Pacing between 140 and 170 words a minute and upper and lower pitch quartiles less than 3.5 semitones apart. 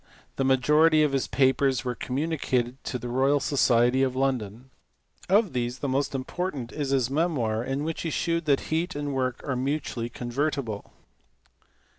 Yes: average, 160 wpm; average, 3.0 semitones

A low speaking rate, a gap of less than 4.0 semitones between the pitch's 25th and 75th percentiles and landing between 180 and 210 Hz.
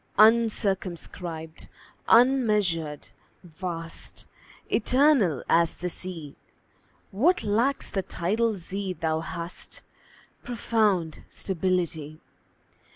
No: slow, 75 wpm; average, 4.9 semitones; medium, 185 Hz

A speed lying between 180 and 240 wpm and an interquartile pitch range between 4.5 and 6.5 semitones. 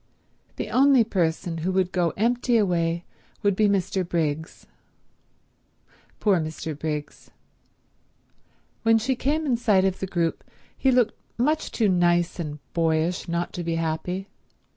No: average, 140 wpm; average, 5.1 semitones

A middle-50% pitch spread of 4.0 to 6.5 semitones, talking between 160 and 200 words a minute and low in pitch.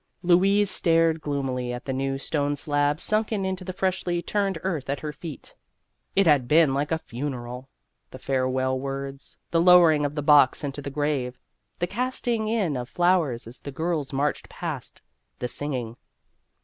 No: average, 4.6 semitones; average, 170 wpm; medium, 145 Hz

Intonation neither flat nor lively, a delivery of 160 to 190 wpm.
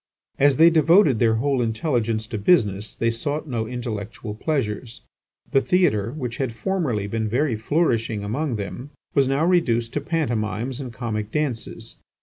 No: average, 4.8 semitones; average, 150 wpm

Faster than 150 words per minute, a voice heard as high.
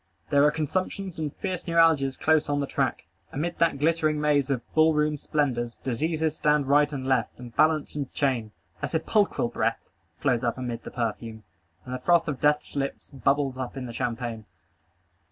No: average, 180 wpm; medium, 145 Hz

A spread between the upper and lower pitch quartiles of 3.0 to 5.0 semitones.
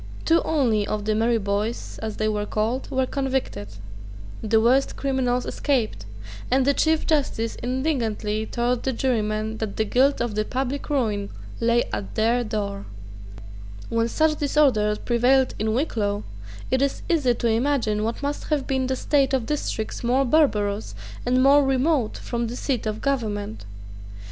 Yes: average, 3.9 semitones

